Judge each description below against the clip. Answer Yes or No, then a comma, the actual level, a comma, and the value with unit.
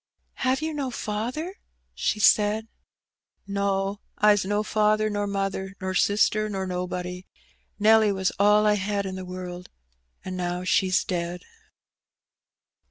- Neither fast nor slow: No, slow, 130 wpm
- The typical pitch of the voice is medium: No, high, 200 Hz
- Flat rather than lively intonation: Yes, narrow, 2.3 semitones